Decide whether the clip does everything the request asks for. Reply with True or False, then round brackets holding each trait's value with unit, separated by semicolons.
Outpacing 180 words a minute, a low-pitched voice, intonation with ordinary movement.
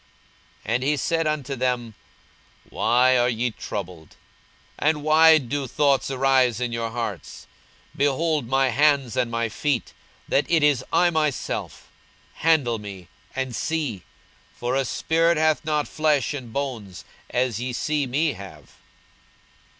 False (140 wpm; 130 Hz; 4.1 semitones)